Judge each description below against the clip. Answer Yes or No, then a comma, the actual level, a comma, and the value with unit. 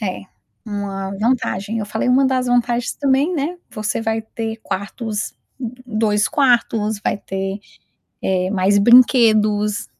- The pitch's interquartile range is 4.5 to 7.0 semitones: No, average, 3.2 semitones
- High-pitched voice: Yes, high, 220 Hz